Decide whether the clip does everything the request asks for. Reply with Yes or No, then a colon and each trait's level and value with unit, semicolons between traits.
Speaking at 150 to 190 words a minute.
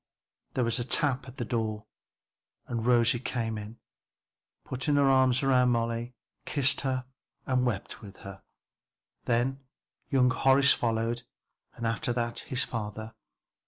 No: slow, 135 wpm